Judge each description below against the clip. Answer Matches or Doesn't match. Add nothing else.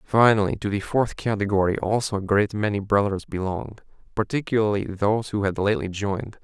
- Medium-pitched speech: Doesn't match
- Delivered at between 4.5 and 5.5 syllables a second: Doesn't match